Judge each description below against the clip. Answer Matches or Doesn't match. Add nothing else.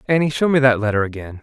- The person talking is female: Doesn't match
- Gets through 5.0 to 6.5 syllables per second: Doesn't match